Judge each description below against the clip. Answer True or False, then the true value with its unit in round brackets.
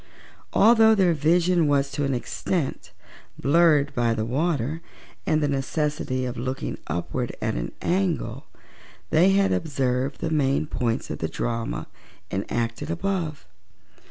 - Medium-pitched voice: True (145 Hz)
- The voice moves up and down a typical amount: True (4.9 semitones)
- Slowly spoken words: True (130 wpm)